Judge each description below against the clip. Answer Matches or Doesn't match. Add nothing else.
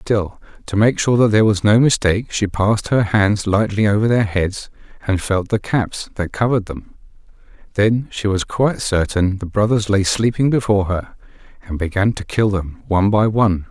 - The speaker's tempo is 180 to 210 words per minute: Matches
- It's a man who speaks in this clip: Matches